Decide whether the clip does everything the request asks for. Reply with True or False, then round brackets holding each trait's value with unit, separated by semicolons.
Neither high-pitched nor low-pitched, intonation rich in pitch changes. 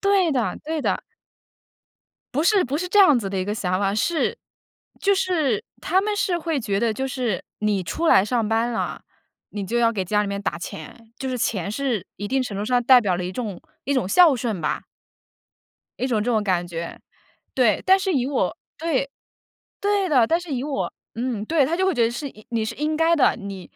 False (245 Hz; 7.0 semitones)